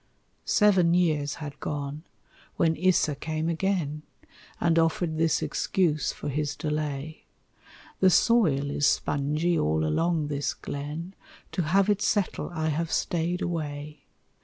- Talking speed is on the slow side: Yes, slow, 130 wpm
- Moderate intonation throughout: Yes, average, 3.0 semitones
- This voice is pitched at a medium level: Yes, medium, 160 Hz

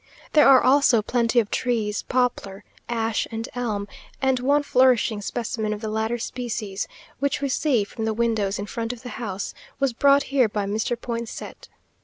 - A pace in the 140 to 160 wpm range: No, average, 175 wpm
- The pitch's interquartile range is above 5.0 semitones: No, average, 3.0 semitones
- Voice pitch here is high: Yes, high, 235 Hz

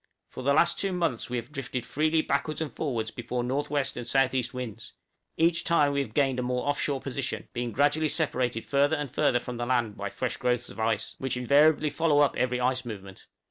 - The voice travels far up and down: No, average, 3.1 semitones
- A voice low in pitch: Yes, low, 130 Hz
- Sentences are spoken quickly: Yes, fast, 215 wpm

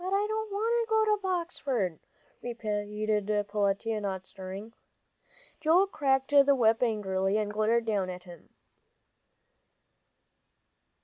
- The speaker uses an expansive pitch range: Yes, wide, 8.7 semitones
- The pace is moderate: No, slow, 115 wpm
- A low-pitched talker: No, high, 225 Hz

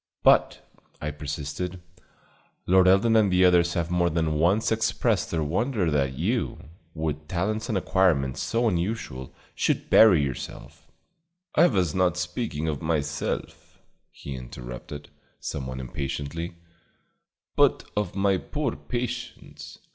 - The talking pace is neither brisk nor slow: No, slow, 125 wpm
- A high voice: No, very low, 85 Hz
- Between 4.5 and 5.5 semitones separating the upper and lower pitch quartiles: Yes, average, 5.2 semitones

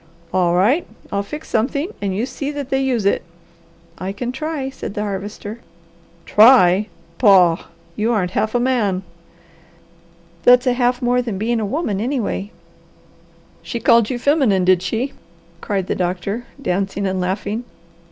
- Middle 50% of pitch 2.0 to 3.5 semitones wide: No, average, 4.5 semitones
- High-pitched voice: Yes, high, 220 Hz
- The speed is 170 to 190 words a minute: No, average, 150 wpm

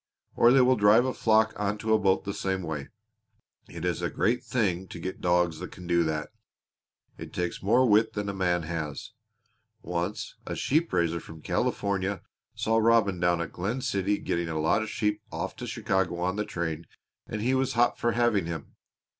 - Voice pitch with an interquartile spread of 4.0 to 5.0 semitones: Yes, average, 4.3 semitones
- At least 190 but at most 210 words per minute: Yes, average, 195 wpm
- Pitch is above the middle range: No, very low, 95 Hz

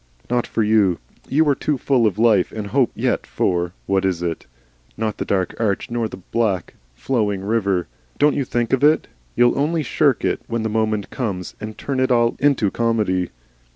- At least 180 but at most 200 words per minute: Yes, average, 190 wpm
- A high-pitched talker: No, low, 110 Hz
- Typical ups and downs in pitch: Yes, average, 4.0 semitones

